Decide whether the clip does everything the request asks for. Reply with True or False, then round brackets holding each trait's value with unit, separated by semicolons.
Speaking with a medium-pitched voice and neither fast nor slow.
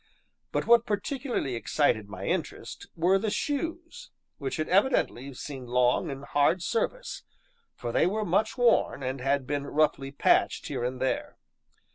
True (155 Hz; 150 wpm)